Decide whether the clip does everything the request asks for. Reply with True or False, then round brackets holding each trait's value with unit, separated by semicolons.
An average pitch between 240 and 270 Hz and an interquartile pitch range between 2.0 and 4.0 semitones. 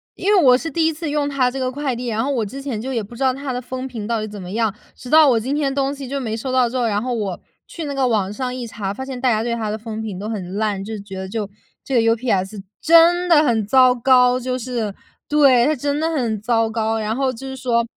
True (250 Hz; 3.7 semitones)